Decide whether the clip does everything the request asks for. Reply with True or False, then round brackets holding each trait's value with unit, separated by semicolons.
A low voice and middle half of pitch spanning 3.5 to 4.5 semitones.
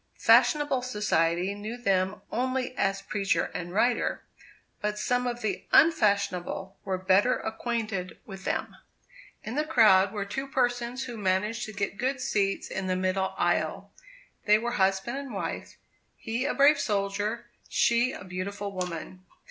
False (210 Hz; 4.2 semitones)